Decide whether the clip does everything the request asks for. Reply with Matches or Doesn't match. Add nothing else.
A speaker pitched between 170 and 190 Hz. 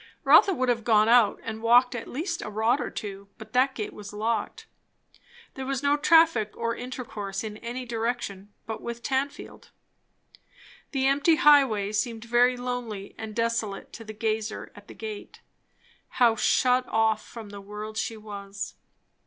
Doesn't match